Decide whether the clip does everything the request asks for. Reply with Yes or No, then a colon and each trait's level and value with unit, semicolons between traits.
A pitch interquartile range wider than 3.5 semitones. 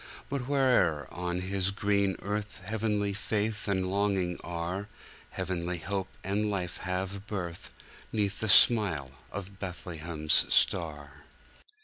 No: average, 2.8 semitones